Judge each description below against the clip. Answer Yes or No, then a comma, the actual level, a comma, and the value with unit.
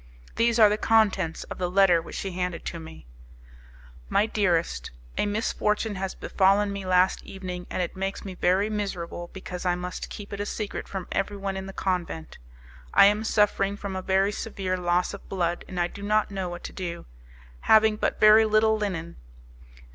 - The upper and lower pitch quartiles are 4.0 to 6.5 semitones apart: No, narrow, 2.4 semitones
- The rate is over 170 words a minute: Yes, average, 185 wpm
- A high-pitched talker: Yes, high, 195 Hz